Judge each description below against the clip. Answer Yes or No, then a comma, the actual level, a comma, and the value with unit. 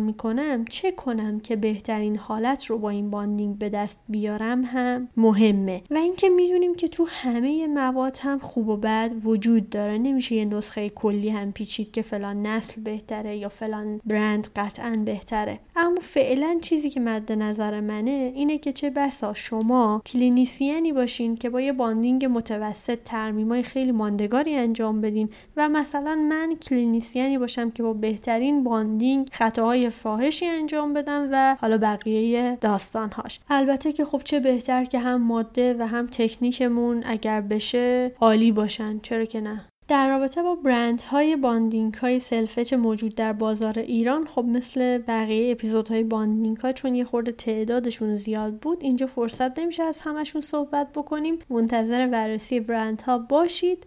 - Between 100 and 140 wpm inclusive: No, fast, 155 wpm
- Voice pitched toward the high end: Yes, high, 235 Hz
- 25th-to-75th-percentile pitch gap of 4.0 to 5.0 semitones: No, average, 3.5 semitones